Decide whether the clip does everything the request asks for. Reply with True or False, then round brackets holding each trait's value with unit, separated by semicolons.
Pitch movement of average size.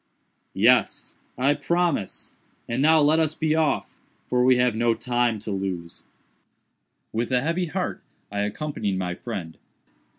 False (7.0 semitones)